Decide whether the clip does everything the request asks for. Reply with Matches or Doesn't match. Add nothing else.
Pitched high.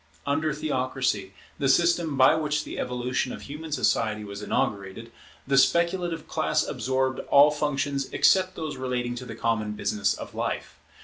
Doesn't match